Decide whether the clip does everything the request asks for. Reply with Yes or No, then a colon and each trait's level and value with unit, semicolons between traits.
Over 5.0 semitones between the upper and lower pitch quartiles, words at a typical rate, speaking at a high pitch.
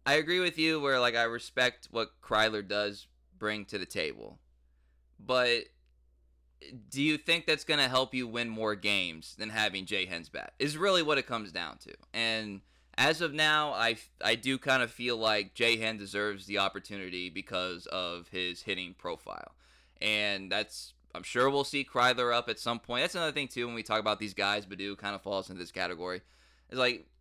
No: wide, 5.4 semitones; average, 195 wpm; low, 105 Hz